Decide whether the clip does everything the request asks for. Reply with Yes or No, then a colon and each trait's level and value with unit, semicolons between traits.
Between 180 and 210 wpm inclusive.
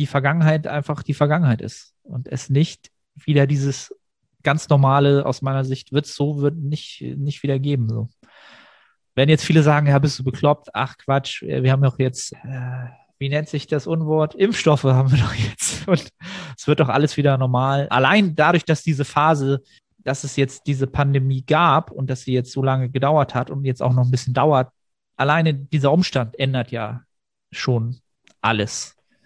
Yes: average, 185 wpm